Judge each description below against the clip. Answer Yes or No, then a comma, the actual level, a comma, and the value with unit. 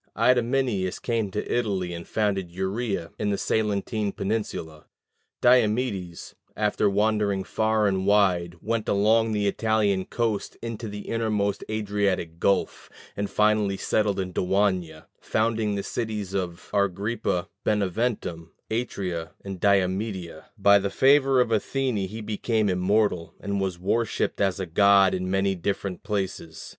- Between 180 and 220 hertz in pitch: No, low, 100 Hz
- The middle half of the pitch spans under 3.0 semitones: Yes, narrow, 2.5 semitones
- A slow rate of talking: Yes, slow, 130 wpm